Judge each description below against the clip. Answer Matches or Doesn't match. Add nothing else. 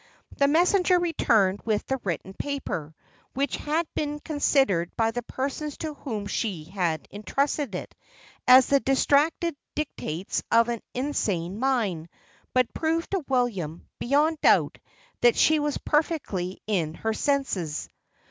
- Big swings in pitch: Matches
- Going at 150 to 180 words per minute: Doesn't match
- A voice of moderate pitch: Doesn't match